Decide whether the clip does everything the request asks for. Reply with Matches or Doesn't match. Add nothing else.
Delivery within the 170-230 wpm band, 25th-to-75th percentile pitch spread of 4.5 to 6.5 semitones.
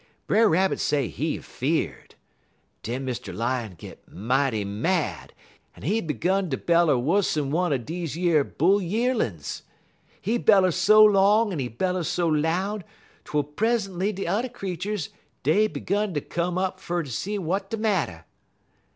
Doesn't match